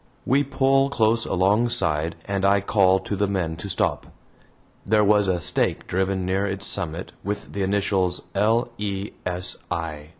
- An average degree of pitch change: No, narrow, 2.3 semitones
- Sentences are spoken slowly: No, average, 160 wpm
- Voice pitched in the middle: No, low, 100 Hz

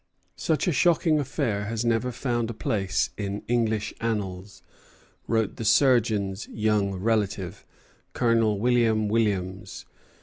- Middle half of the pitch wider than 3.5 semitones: No, average, 2.7 semitones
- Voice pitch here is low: Yes, low, 110 Hz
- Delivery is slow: Yes, slow, 115 wpm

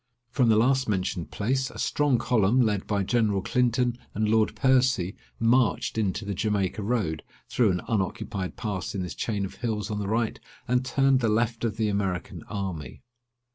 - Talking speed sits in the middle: Yes, average, 175 wpm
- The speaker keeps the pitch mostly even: No, average, 3.8 semitones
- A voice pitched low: Yes, low, 110 Hz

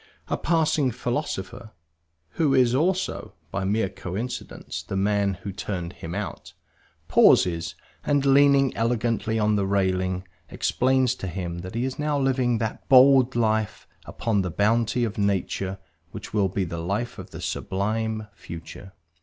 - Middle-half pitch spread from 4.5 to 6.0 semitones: Yes, average, 4.8 semitones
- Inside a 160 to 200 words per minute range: No, average, 150 wpm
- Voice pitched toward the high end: No, low, 110 Hz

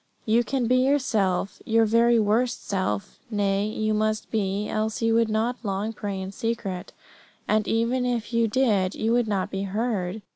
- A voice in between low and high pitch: No, high, 220 Hz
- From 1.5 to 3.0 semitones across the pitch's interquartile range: Yes, narrow, 2.6 semitones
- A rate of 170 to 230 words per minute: Yes, average, 175 wpm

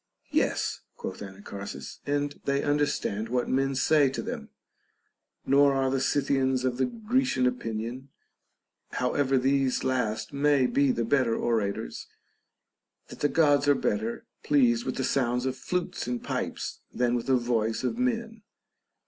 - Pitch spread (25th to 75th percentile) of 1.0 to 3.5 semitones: Yes, average, 3.1 semitones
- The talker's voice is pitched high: No, low, 130 Hz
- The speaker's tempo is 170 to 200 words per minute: No, average, 150 wpm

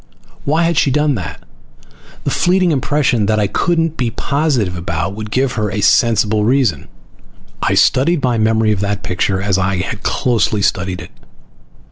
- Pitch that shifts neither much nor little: No, wide, 5.9 semitones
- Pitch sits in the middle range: No, low, 110 Hz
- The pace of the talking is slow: No, average, 165 wpm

